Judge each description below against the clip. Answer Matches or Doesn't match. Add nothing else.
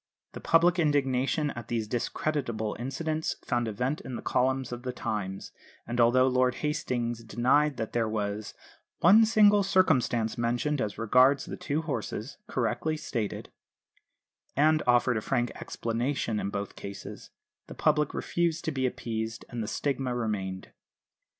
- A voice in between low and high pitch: Doesn't match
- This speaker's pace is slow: Doesn't match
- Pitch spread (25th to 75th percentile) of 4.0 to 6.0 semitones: Matches